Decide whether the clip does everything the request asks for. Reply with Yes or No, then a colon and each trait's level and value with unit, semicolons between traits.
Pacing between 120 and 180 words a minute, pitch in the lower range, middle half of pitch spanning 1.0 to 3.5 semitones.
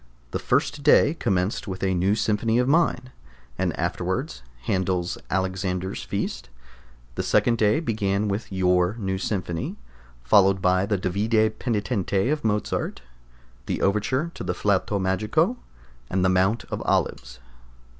Yes: slow, 135 wpm; low, 100 Hz; average, 2.9 semitones